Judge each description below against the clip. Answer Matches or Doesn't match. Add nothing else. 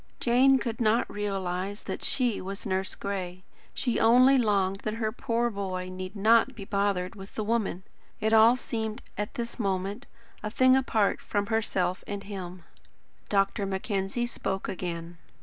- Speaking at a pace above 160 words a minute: Doesn't match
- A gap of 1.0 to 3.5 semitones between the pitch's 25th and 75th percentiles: Matches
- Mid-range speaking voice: Doesn't match